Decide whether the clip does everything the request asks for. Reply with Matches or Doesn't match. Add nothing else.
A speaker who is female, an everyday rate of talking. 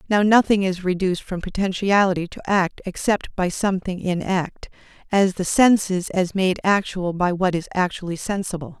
Matches